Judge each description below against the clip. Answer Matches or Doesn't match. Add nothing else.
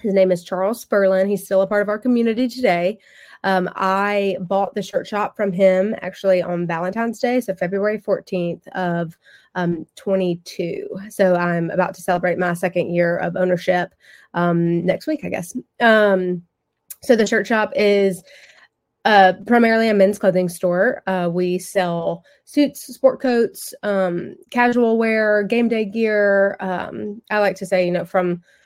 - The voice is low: Doesn't match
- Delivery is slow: Doesn't match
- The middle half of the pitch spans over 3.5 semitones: Doesn't match